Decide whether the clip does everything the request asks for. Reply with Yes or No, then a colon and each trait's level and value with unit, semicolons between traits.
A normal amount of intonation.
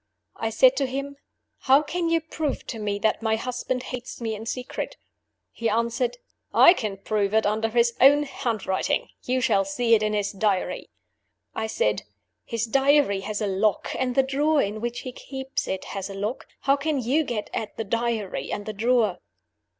Yes: average, 3.9 semitones